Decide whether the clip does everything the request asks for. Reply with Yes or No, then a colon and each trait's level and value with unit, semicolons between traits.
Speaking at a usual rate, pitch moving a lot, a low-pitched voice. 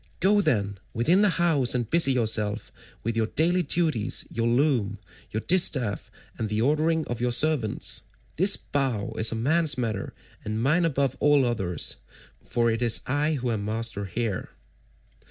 Yes: average, 160 wpm; wide, 5.7 semitones; low, 120 Hz